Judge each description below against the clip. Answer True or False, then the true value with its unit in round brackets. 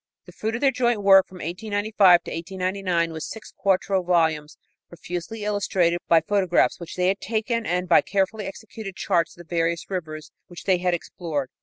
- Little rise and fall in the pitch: False (3.0 semitones)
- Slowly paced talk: False (180 wpm)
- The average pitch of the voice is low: False (185 Hz)